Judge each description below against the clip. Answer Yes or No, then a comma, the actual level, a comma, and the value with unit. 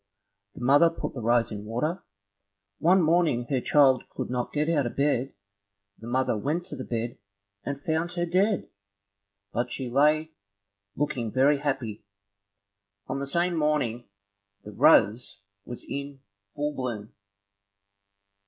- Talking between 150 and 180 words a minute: No, average, 140 wpm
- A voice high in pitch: No, medium, 140 Hz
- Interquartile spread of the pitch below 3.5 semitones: No, average, 4.2 semitones